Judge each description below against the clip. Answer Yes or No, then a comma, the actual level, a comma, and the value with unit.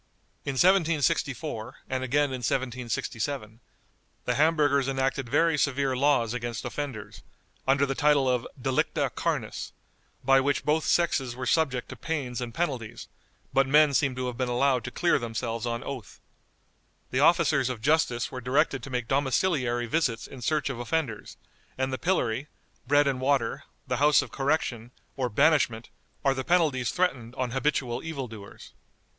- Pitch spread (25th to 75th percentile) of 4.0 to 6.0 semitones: No, average, 3.2 semitones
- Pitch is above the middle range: No, low, 130 Hz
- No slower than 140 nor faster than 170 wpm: Yes, average, 155 wpm